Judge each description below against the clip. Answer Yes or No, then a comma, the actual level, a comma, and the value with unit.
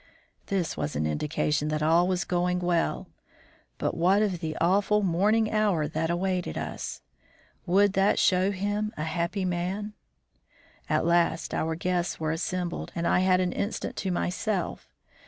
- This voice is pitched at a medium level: Yes, medium, 180 Hz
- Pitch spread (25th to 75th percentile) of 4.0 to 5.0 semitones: No, average, 2.8 semitones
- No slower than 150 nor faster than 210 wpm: Yes, average, 155 wpm